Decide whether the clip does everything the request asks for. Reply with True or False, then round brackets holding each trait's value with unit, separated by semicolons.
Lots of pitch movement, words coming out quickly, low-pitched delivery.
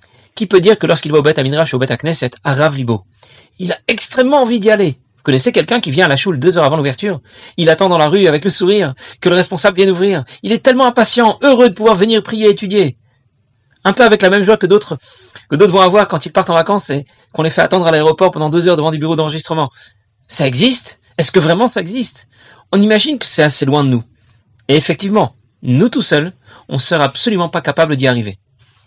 False (7.4 semitones; 245 wpm; 165 Hz)